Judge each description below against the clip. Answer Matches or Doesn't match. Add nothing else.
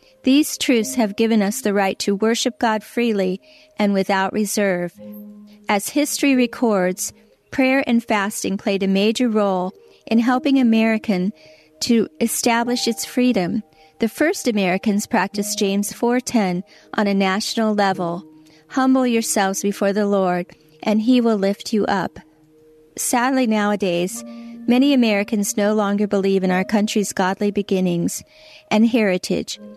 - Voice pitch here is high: Matches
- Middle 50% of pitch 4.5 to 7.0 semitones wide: Doesn't match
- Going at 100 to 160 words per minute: Matches